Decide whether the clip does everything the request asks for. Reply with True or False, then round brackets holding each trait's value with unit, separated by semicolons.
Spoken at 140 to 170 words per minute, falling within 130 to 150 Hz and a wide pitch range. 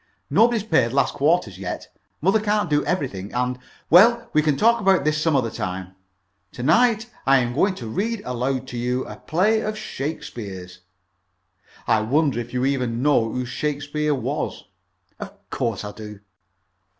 True (165 wpm; 140 Hz; 7.2 semitones)